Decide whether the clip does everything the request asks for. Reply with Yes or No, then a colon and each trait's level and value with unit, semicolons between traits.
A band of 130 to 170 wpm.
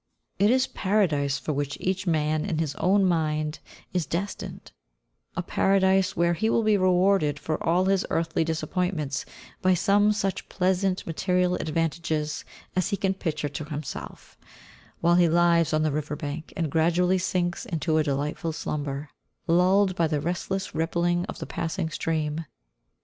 Yes: average, 155 wpm